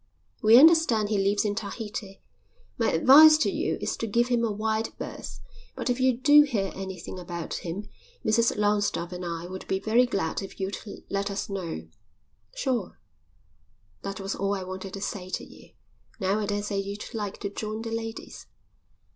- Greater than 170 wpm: Yes, average, 180 wpm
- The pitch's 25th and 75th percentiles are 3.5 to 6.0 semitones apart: No, average, 2.8 semitones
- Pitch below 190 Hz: No, high, 205 Hz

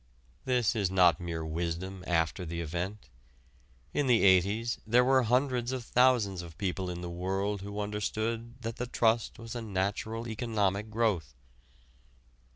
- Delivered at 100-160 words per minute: Yes, average, 150 wpm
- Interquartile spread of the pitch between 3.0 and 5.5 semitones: Yes, average, 4.4 semitones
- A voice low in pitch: Yes, low, 105 Hz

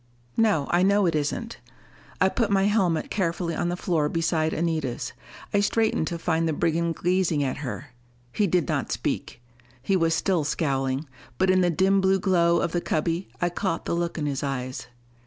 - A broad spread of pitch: No, average, 3.3 semitones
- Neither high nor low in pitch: Yes, medium, 170 Hz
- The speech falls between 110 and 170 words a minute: No, average, 190 wpm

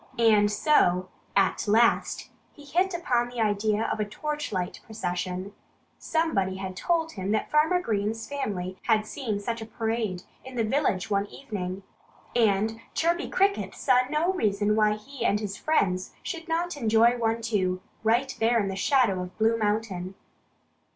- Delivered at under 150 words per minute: No, average, 155 wpm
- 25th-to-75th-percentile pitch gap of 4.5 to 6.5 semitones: Yes, average, 4.9 semitones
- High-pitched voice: Yes, high, 220 Hz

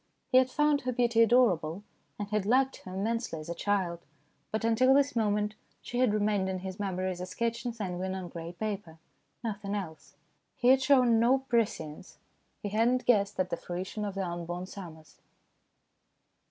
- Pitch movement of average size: Yes, average, 4.3 semitones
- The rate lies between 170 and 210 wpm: Yes, average, 180 wpm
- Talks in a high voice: Yes, high, 205 Hz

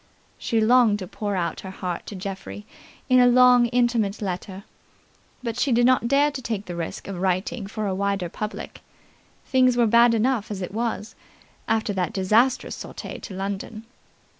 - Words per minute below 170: No, average, 175 wpm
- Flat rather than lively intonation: No, average, 3.8 semitones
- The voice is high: Yes, high, 215 Hz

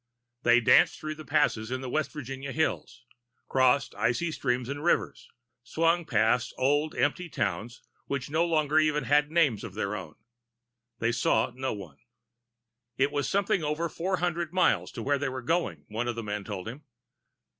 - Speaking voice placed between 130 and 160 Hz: Yes, low, 135 Hz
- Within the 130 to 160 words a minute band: No, average, 175 wpm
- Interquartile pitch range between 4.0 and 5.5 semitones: Yes, average, 4.7 semitones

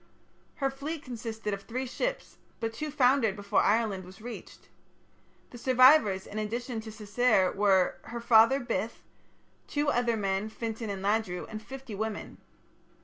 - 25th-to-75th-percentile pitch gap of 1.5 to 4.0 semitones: Yes, average, 3.5 semitones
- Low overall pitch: No, high, 225 Hz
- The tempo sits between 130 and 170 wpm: Yes, average, 145 wpm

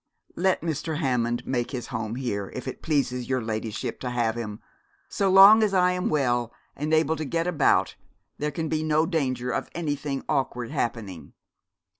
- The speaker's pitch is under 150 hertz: Yes, low, 135 Hz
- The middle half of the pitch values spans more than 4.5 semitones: Yes, average, 5.0 semitones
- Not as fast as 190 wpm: Yes, average, 175 wpm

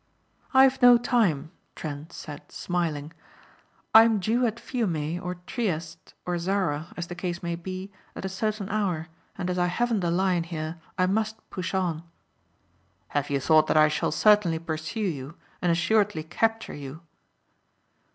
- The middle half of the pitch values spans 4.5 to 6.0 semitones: Yes, average, 4.8 semitones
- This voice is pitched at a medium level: Yes, medium, 180 Hz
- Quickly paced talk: No, average, 160 wpm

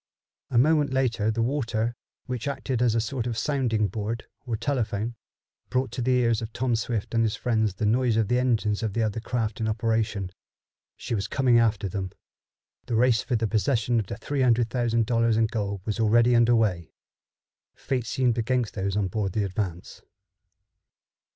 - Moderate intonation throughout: No, narrow, 2.3 semitones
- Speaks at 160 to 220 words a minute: Yes, average, 185 wpm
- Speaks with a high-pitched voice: No, low, 115 Hz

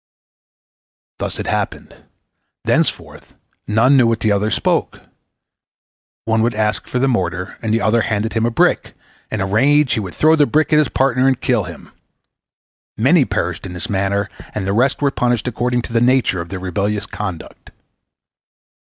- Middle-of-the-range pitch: No, low, 115 Hz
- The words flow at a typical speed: Yes, average, 175 wpm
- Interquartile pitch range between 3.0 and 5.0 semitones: Yes, average, 3.7 semitones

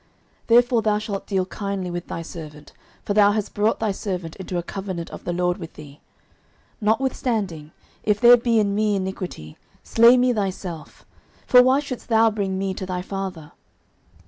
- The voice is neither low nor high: No, high, 195 Hz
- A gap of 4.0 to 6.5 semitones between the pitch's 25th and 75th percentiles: No, average, 3.6 semitones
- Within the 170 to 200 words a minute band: Yes, average, 175 wpm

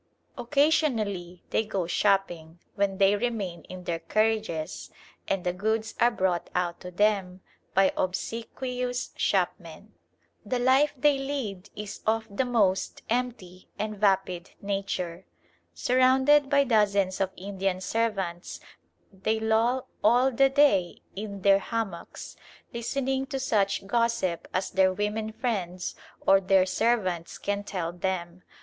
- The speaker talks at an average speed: No, slow, 130 wpm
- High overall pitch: Yes, high, 205 Hz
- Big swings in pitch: No, average, 4.2 semitones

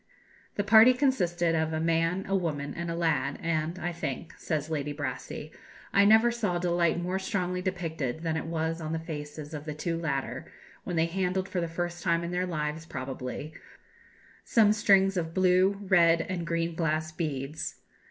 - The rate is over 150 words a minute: Yes, average, 180 wpm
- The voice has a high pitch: No, medium, 170 Hz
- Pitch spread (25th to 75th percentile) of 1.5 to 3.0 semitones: Yes, narrow, 2.5 semitones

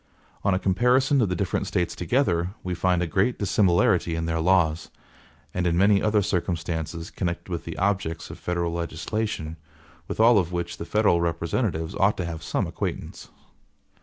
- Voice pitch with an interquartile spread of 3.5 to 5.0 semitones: No, average, 3.1 semitones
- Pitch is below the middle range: Yes, very low, 90 Hz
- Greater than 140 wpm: Yes, average, 170 wpm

